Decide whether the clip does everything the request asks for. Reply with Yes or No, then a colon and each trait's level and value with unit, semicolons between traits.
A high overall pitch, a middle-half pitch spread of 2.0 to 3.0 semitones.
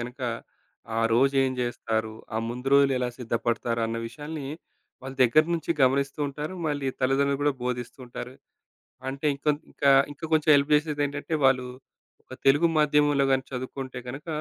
No: low, 135 Hz; average, 2.7 semitones